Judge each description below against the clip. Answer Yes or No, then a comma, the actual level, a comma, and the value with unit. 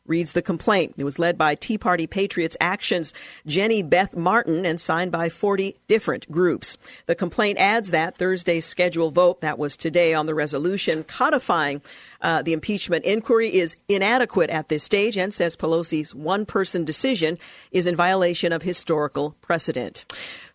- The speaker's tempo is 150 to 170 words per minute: Yes, average, 160 wpm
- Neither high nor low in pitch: Yes, medium, 175 Hz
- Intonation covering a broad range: No, average, 3.1 semitones